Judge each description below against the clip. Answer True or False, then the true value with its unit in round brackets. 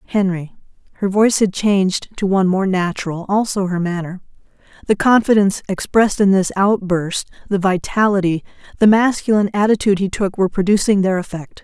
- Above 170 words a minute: False (145 wpm)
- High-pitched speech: True (195 Hz)